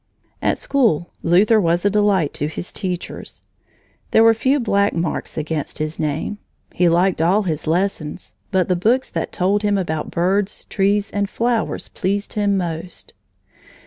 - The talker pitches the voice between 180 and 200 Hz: Yes, high, 190 Hz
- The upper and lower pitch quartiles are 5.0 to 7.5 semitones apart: No, average, 3.6 semitones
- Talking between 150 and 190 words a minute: Yes, average, 155 wpm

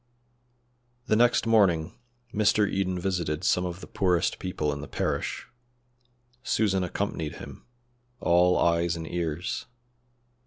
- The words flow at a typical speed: No, slow, 120 wpm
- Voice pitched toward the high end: No, very low, 90 Hz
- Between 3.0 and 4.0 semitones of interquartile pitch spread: No, narrow, 2.6 semitones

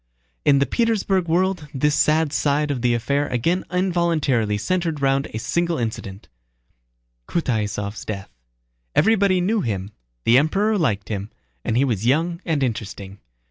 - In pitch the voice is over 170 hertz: No, medium, 140 Hz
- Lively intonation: Yes, wide, 7.3 semitones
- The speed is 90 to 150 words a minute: Yes, average, 140 wpm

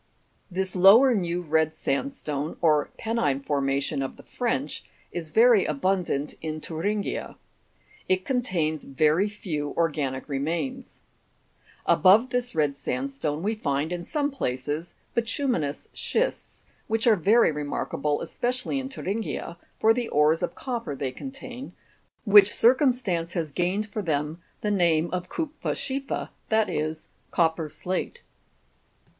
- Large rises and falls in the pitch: Yes, wide, 6.9 semitones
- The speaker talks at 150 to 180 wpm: No, slow, 135 wpm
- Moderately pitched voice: Yes, medium, 175 Hz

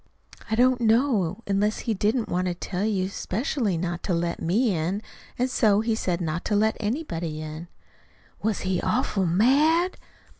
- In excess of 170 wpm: No, average, 165 wpm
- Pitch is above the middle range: Yes, high, 205 Hz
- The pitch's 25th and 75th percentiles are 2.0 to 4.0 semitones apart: No, average, 4.7 semitones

